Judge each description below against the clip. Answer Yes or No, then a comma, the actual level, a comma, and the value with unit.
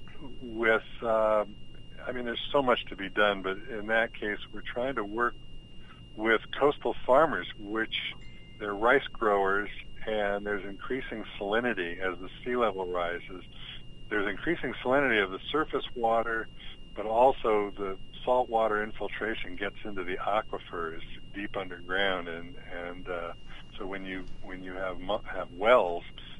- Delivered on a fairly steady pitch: No, average, 3.3 semitones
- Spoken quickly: No, average, 145 wpm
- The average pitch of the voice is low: Yes, low, 105 Hz